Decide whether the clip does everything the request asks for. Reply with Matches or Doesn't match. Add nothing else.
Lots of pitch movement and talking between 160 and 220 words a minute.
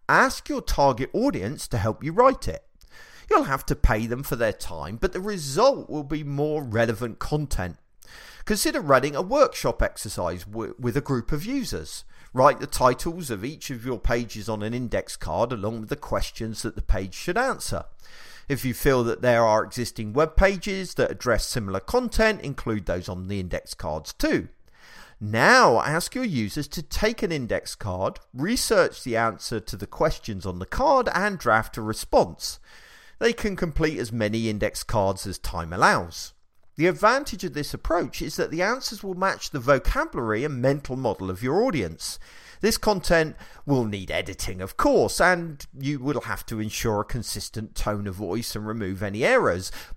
Matches